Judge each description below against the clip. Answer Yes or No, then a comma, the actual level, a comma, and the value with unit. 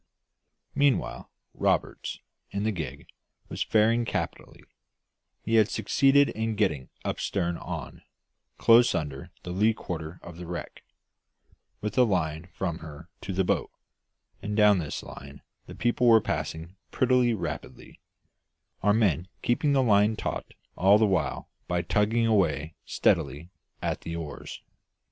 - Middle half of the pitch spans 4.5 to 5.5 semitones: Yes, average, 5.0 semitones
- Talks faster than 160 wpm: No, average, 140 wpm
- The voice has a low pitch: Yes, low, 100 Hz